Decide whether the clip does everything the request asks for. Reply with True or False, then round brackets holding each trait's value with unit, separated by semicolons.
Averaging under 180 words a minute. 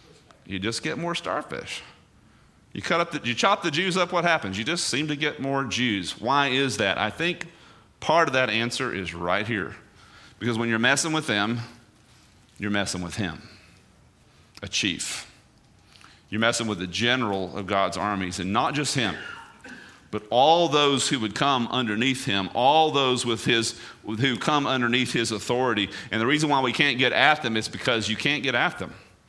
False (190 wpm)